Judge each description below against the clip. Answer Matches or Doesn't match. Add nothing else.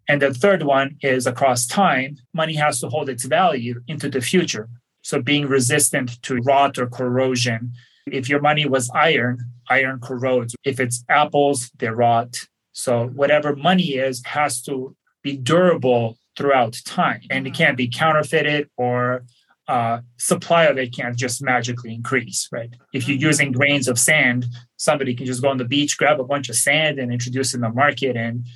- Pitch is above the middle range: Doesn't match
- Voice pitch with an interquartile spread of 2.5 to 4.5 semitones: Matches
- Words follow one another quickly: Doesn't match